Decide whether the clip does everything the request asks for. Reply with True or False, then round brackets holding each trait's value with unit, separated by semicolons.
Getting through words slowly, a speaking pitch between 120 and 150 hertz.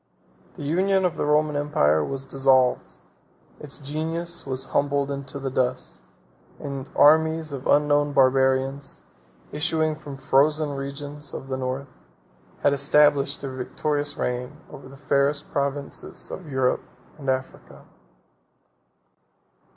True (125 wpm; 140 Hz)